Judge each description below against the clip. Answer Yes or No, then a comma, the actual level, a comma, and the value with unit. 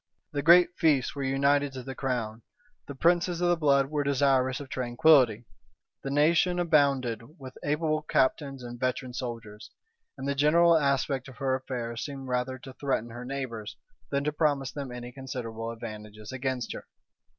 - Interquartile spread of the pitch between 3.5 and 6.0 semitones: No, average, 2.8 semitones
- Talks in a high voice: No, low, 135 Hz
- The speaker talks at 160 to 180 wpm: Yes, average, 165 wpm